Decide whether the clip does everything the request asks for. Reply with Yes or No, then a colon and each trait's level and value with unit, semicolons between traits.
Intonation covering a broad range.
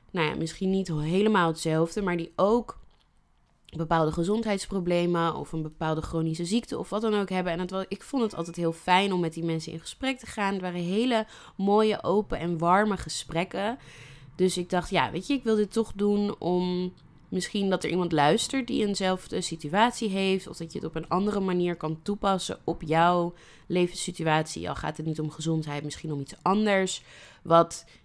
No: average, 3.5 semitones